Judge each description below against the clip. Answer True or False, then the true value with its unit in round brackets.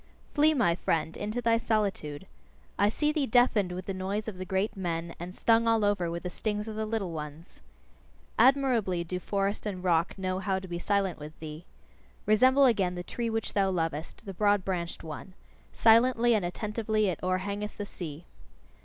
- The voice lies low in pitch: False (195 Hz)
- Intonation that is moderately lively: True (3.8 semitones)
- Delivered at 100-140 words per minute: False (185 wpm)